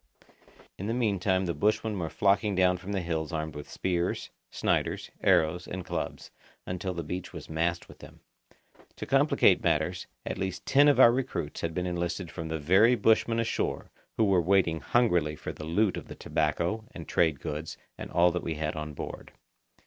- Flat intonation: No, average, 3.4 semitones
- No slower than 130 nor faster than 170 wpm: No, average, 185 wpm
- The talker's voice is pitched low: Yes, very low, 90 Hz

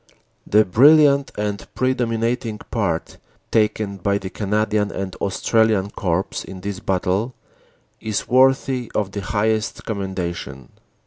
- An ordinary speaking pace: No, slow, 120 wpm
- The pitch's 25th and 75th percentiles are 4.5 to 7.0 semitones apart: No, average, 3.0 semitones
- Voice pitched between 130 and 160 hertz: No, low, 105 Hz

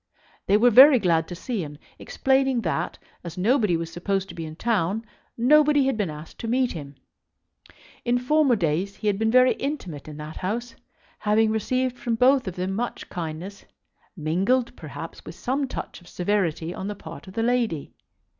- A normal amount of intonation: No, wide, 6.4 semitones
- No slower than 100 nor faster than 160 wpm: No, average, 185 wpm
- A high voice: Yes, high, 210 Hz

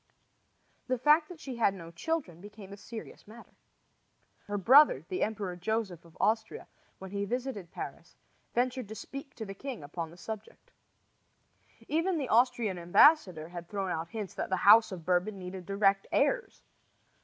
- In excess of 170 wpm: No, average, 165 wpm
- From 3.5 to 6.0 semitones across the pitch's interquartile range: Yes, wide, 5.4 semitones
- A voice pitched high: Yes, high, 205 Hz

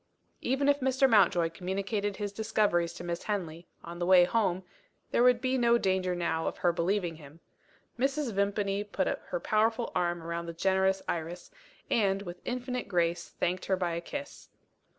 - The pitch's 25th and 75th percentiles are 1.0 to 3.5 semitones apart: No, average, 4.5 semitones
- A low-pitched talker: No, high, 190 Hz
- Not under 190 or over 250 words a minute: No, average, 170 wpm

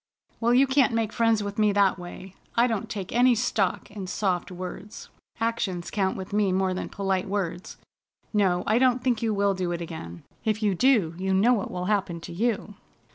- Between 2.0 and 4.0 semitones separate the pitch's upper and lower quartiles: Yes, average, 3.5 semitones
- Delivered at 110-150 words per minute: No, average, 200 wpm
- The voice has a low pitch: No, high, 200 Hz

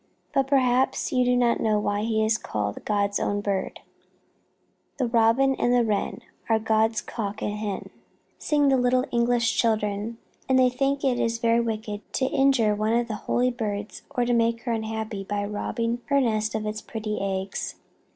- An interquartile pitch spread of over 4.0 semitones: No, average, 2.7 semitones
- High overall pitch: Yes, high, 225 Hz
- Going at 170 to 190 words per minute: Yes, average, 180 wpm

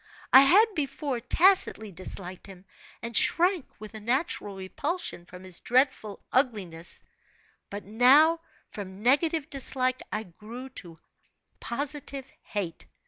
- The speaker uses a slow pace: Yes, slow, 120 wpm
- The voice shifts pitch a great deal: Yes, wide, 6.0 semitones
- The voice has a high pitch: Yes, high, 240 Hz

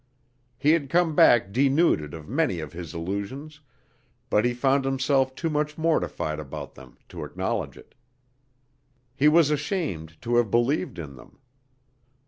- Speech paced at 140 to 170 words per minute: Yes, average, 145 wpm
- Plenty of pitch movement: Yes, wide, 8.5 semitones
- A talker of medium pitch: No, low, 130 Hz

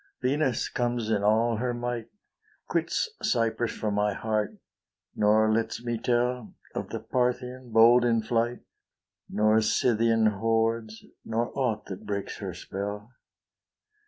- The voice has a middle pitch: No, low, 115 Hz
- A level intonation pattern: Yes, narrow, 2.0 semitones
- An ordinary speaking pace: No, slow, 130 wpm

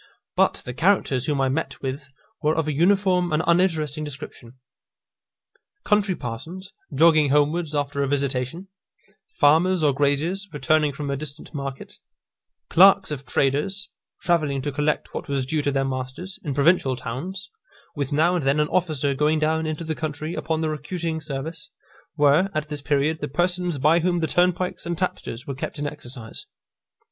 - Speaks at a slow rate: No, average, 165 wpm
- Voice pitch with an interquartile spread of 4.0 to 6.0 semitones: No, average, 3.5 semitones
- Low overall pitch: No, medium, 150 Hz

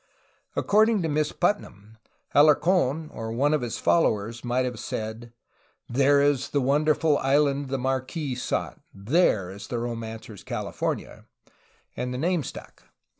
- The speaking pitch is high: No, low, 135 Hz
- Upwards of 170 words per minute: No, average, 145 wpm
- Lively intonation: No, average, 4.5 semitones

